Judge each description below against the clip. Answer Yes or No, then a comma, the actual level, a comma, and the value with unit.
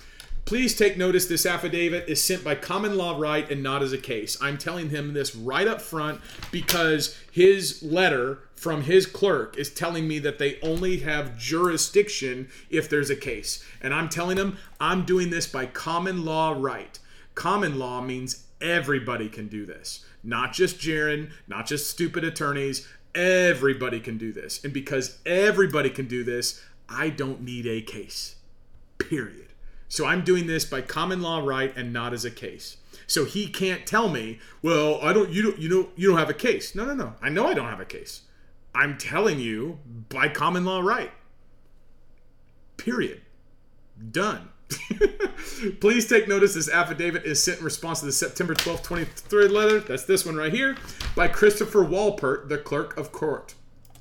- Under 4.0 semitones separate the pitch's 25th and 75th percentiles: No, average, 5.1 semitones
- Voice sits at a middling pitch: Yes, medium, 160 Hz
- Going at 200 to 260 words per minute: No, average, 175 wpm